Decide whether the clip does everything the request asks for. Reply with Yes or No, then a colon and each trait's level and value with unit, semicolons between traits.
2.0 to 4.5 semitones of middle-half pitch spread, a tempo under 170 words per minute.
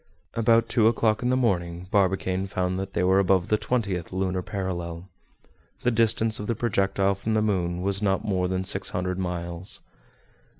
No: average, 2.9 semitones; average, 175 wpm